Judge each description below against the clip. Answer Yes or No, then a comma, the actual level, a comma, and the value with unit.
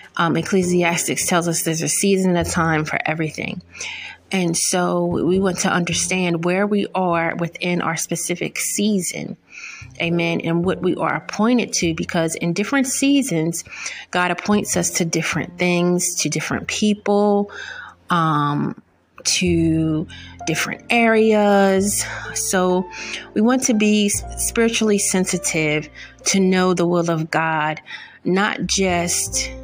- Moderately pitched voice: Yes, medium, 180 Hz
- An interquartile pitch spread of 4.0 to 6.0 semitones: No, average, 3.4 semitones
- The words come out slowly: Yes, slow, 130 wpm